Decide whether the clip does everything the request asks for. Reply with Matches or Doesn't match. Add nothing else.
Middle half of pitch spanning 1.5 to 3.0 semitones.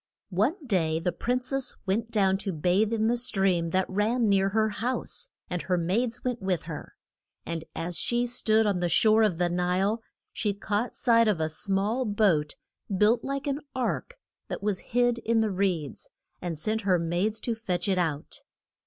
Doesn't match